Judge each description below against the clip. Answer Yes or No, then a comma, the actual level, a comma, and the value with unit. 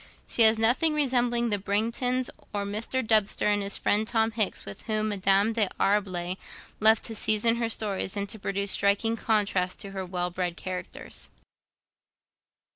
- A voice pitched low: No, high, 210 Hz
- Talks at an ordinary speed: Yes, average, 155 wpm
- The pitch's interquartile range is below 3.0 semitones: Yes, narrow, 2.4 semitones